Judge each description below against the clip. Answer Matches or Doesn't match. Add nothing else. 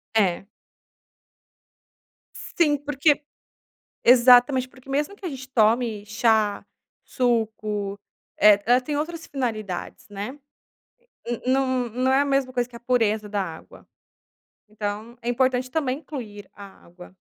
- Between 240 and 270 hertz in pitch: Matches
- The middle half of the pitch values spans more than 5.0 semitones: Doesn't match